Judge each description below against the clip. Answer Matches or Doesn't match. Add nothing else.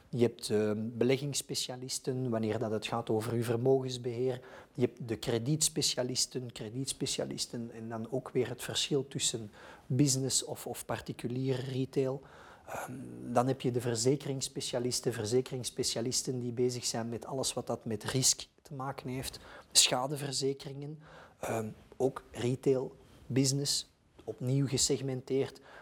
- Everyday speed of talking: Doesn't match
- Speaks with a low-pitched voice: Matches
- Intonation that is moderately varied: Doesn't match